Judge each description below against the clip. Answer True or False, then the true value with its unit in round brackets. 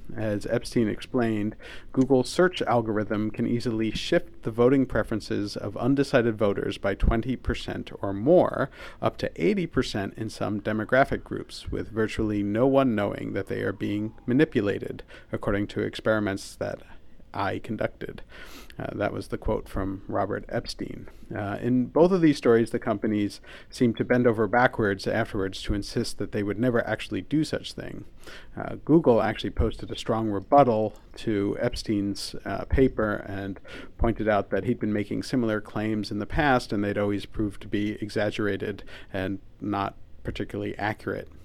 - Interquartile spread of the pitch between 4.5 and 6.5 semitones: False (2.7 semitones)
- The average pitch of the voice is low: True (110 Hz)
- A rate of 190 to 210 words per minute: False (155 wpm)